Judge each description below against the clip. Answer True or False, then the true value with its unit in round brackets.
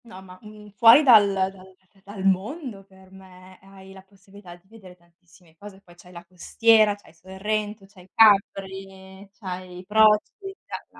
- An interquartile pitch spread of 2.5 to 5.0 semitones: False (2.1 semitones)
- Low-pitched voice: False (195 Hz)